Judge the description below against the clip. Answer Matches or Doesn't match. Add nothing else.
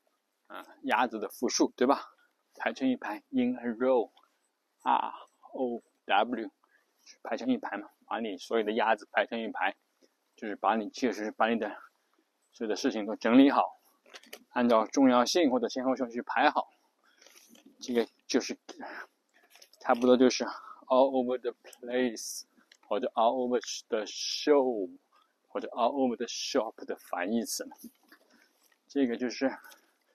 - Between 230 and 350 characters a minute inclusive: Matches